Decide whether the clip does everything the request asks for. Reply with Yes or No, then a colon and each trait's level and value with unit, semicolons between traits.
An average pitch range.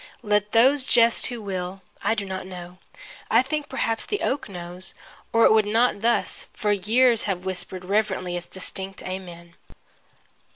Yes: average, 3.8 semitones